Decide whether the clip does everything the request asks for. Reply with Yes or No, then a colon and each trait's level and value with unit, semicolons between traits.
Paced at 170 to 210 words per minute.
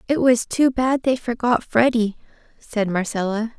No: average, 150 wpm